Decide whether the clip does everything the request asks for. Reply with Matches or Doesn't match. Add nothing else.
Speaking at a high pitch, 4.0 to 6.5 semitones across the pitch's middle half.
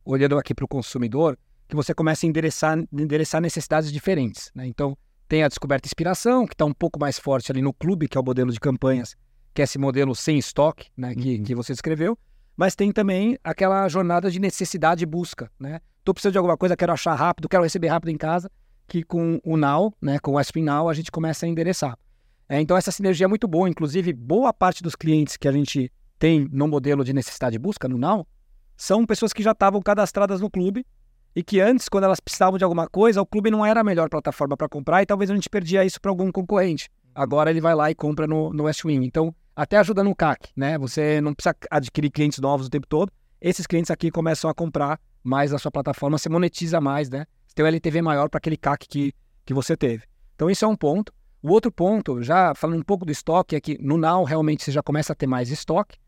Doesn't match